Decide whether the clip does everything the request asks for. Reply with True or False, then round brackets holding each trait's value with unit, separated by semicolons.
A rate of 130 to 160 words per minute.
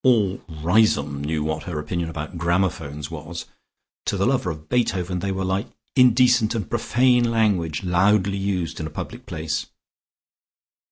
True (150 wpm)